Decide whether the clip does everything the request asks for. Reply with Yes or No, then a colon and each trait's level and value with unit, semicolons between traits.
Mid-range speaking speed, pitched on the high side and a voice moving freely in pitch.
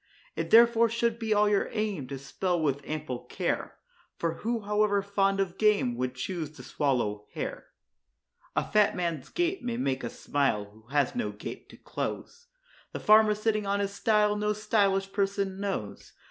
Yes: average, 175 wpm; high, 200 Hz; wide, 6.8 semitones